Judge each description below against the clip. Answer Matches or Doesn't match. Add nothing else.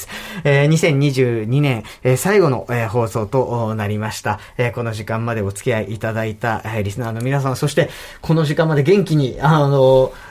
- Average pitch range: Matches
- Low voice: Matches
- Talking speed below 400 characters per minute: Matches